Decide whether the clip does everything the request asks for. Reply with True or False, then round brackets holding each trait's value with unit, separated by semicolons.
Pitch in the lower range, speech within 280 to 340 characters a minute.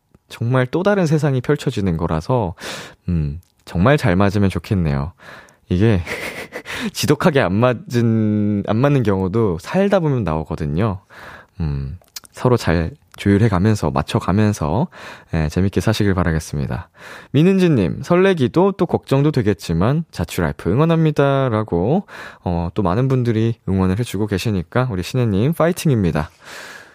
True (105 Hz; 295 characters per minute)